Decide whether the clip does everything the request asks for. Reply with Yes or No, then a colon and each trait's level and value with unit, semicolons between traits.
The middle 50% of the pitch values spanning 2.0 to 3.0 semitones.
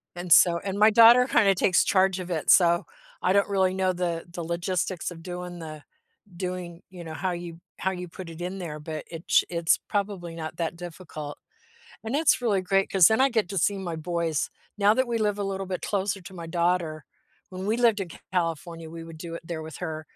Yes: average, 2.7 semitones